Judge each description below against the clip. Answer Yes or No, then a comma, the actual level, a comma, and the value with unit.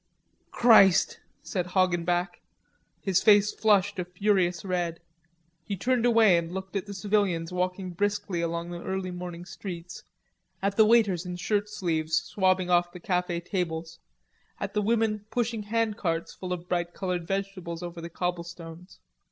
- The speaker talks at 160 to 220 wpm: No, average, 150 wpm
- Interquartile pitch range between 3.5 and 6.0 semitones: No, average, 2.7 semitones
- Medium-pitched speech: Yes, medium, 180 Hz